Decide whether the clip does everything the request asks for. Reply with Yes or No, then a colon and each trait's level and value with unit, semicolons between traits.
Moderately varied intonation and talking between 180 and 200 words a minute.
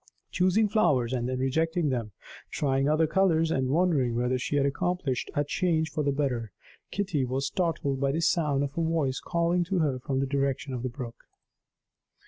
Yes: average, 4.1 semitones; average, 185 wpm